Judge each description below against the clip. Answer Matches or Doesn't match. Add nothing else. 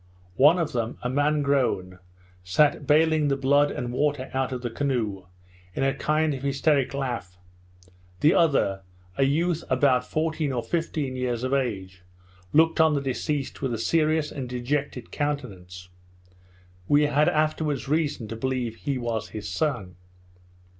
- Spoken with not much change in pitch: Doesn't match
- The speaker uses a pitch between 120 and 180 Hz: Matches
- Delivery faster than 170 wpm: Doesn't match